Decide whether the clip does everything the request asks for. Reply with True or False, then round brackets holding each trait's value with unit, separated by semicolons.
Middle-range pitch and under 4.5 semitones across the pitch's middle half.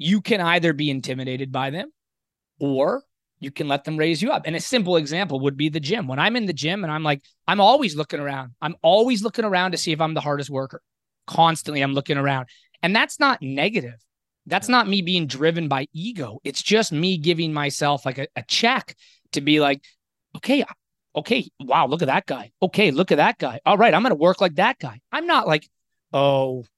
False (155 Hz; 5.1 semitones)